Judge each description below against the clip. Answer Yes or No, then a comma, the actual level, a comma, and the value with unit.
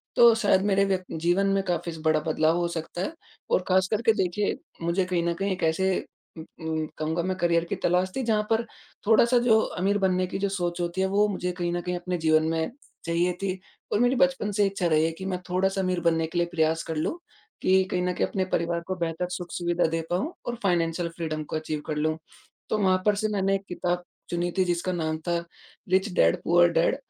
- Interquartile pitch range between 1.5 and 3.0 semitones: Yes, narrow, 2.4 semitones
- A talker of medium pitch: Yes, medium, 180 Hz